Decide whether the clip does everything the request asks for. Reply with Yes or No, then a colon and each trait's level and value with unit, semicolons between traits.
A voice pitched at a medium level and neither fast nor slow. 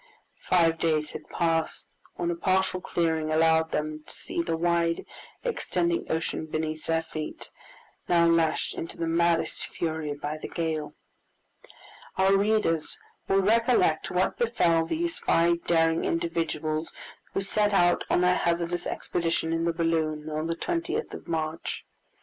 Yes: medium, 165 Hz; average, 145 wpm